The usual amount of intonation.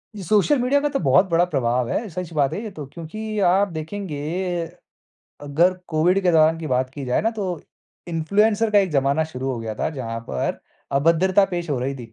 No: wide, 6.3 semitones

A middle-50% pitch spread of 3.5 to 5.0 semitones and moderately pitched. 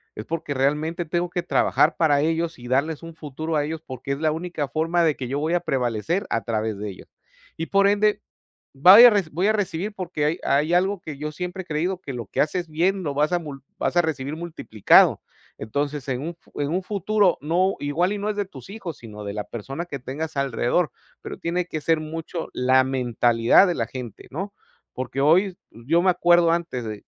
Yes: average, 4.6 semitones; medium, 160 Hz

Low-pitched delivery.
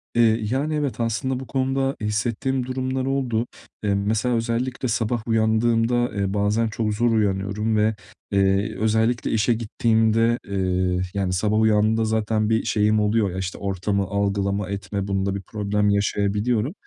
Yes: low, 110 Hz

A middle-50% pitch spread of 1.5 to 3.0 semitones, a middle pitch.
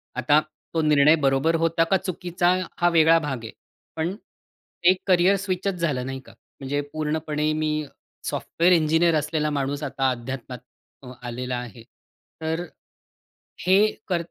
No: average, 3.8 semitones; medium, 155 Hz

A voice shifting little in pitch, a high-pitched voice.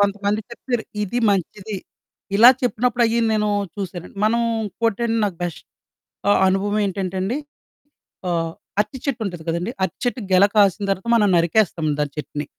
No: average, 3.5 semitones; high, 205 Hz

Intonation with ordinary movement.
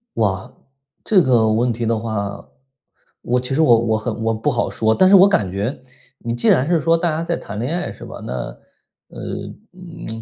No: wide, 6.9 semitones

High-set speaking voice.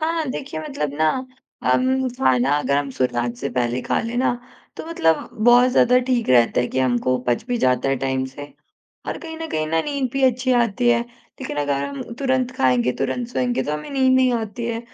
Yes: high, 230 Hz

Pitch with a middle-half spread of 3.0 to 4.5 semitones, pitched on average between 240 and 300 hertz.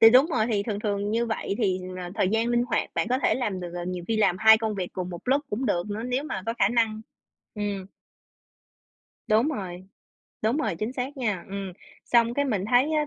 No: average, 3.9 semitones; high, 215 Hz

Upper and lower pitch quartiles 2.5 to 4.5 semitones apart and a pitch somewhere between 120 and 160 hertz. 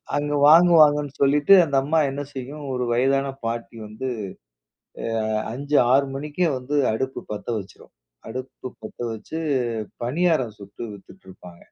Yes: average, 4.2 semitones; low, 135 Hz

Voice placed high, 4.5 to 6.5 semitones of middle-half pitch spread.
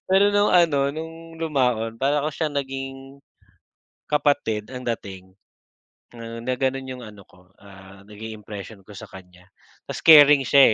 No: low, 130 Hz; wide, 5.6 semitones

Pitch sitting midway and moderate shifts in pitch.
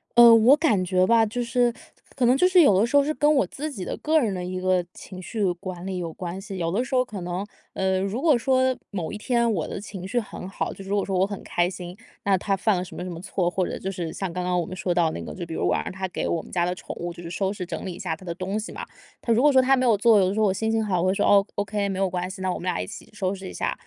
No: high, 195 Hz; average, 4.0 semitones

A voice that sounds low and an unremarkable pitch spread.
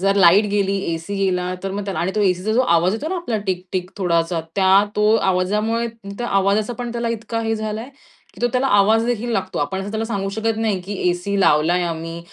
No: high, 200 Hz; average, 3.4 semitones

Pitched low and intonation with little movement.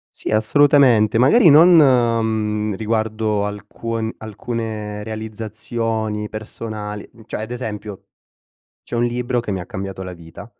Yes: low, 110 Hz; narrow, 2.0 semitones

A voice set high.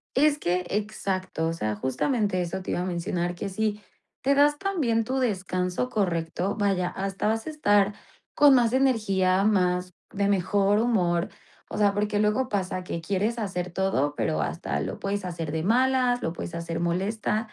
Yes: high, 195 Hz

